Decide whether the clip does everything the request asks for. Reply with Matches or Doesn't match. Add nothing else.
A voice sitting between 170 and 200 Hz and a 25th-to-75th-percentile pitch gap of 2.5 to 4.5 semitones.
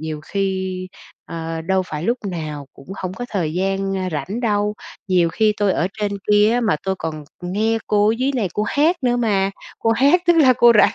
Matches